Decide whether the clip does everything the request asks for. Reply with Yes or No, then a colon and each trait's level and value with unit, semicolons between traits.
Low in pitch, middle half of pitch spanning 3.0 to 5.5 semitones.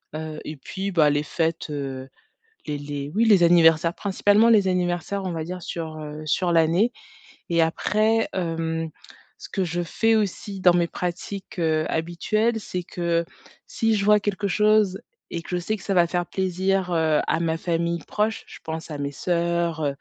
No: medium, 175 Hz; average, 3.4 semitones